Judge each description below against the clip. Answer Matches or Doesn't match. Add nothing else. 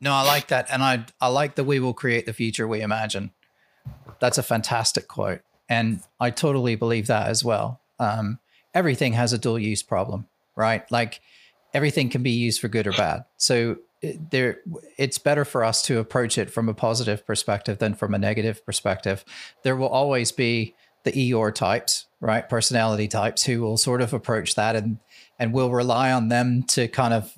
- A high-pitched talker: Doesn't match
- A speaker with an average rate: Matches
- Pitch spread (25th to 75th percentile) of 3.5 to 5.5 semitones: Doesn't match